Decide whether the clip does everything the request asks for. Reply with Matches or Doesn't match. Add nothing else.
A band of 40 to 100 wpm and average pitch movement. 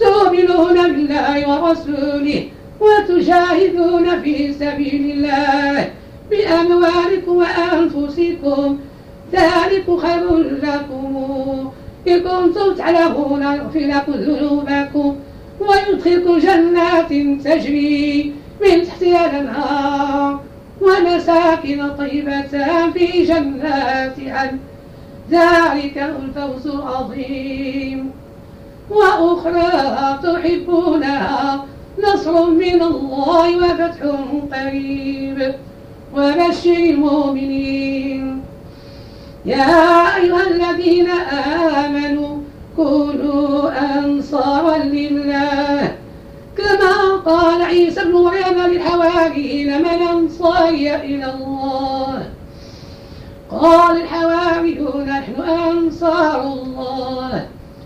Matches